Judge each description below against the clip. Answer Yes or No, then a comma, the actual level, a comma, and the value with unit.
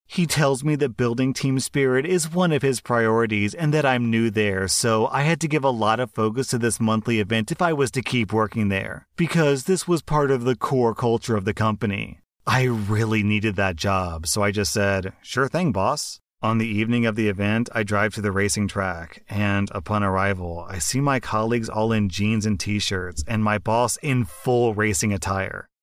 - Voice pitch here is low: Yes, low, 110 Hz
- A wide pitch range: No, average, 4.0 semitones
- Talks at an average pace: No, fast, 215 wpm